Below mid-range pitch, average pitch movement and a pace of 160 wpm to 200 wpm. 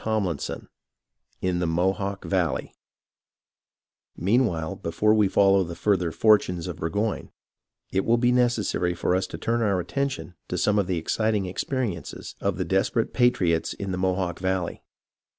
No: very low, 95 Hz; average, 3.5 semitones; average, 150 wpm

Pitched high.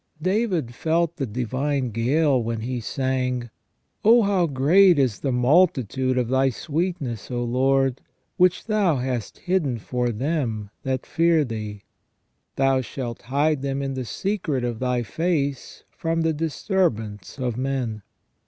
No: low, 135 Hz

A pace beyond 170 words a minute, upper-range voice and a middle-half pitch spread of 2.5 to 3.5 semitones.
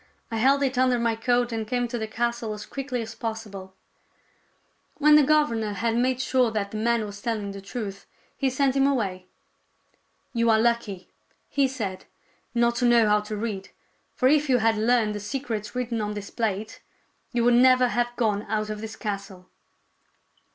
Yes: average, 190 wpm; high, 230 Hz; average, 2.9 semitones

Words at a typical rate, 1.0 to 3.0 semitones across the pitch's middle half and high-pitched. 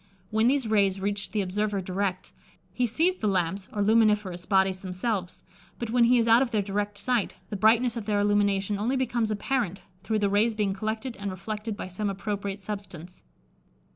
Yes: average, 185 wpm; narrow, 2.4 semitones; high, 205 Hz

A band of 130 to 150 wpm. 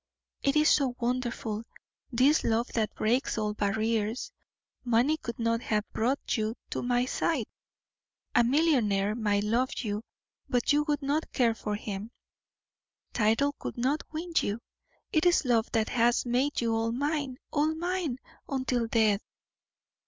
Yes: average, 145 wpm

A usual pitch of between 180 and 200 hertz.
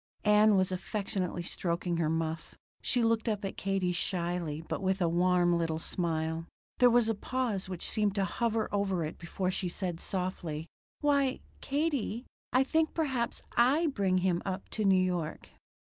Yes: high, 190 Hz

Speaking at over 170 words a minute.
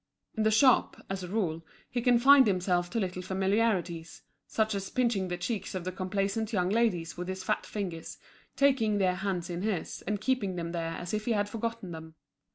Yes: average, 195 wpm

